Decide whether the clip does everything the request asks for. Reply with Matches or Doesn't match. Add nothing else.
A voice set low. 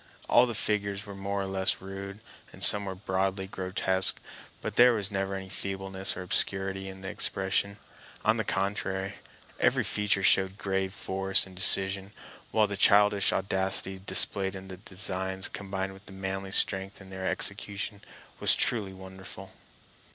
Matches